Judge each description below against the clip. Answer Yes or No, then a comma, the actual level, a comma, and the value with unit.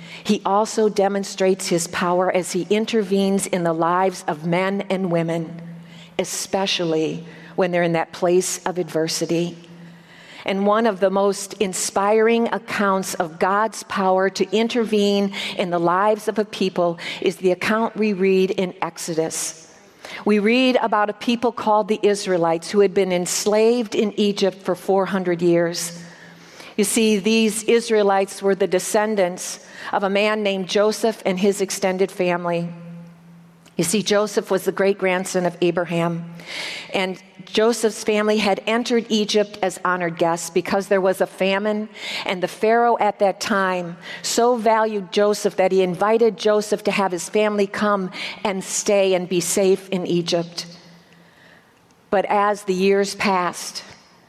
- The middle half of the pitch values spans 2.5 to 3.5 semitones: Yes, average, 2.8 semitones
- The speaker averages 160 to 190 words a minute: No, average, 150 wpm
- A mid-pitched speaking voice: No, high, 195 Hz